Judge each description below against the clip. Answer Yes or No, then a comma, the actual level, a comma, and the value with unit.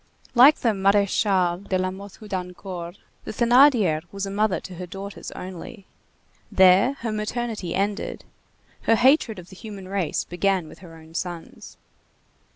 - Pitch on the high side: Yes, high, 195 Hz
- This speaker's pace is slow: No, average, 150 wpm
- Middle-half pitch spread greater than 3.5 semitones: No, average, 2.9 semitones